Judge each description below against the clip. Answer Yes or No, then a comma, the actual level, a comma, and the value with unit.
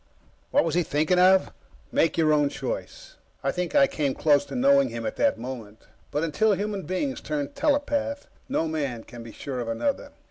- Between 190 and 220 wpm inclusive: Yes, average, 200 wpm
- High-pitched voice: No, medium, 165 Hz